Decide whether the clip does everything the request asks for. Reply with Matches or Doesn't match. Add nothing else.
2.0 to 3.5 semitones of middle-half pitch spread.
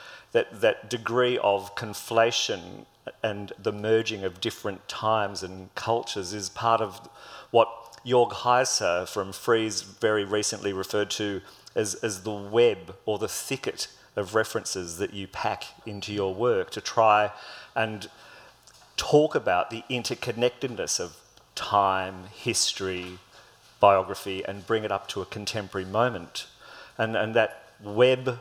Matches